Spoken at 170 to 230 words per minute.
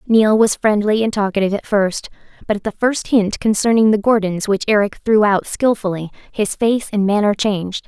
Yes: average, 190 wpm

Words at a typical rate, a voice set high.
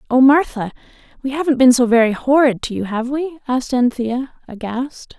Yes: average, 175 wpm; very high, 255 Hz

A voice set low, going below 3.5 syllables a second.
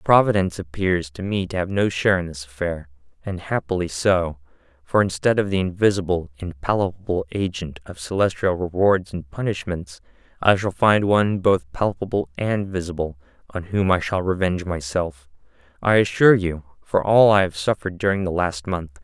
No: very low, 90 Hz; 5.2 syllables/s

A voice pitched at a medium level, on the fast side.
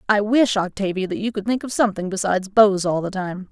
No: high, 200 Hz; fast, 240 wpm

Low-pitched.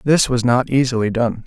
Yes: low, 125 Hz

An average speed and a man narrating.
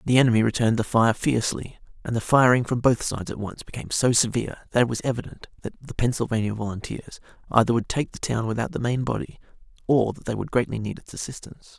No: fast, 210 wpm; male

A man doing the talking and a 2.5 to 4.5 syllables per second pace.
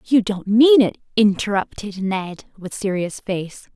No: female; 4.0 syllables/s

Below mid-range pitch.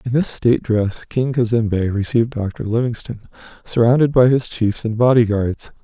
Yes: low, 115 Hz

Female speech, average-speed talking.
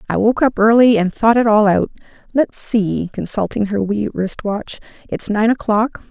Yes: female; average, 185 wpm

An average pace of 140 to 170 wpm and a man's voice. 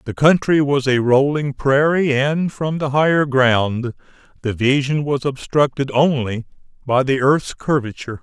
Yes: average, 145 wpm; male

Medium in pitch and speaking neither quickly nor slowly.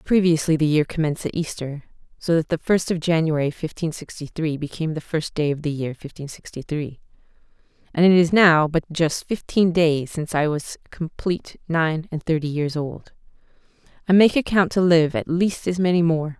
Yes: medium, 160 Hz; average, 185 wpm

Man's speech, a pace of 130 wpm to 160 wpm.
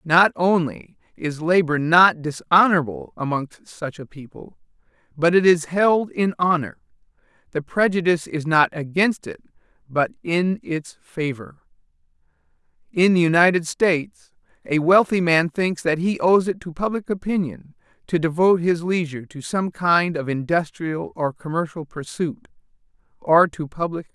Yes: male; average, 140 wpm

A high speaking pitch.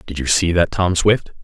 No: very low, 90 Hz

